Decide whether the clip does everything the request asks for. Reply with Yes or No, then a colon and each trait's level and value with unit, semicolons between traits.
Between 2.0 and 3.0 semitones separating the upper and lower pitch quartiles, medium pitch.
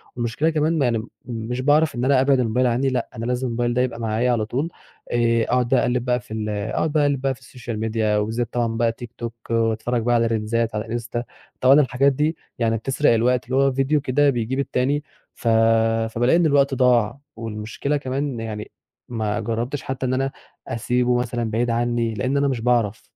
No: average, 2.7 semitones; low, 120 Hz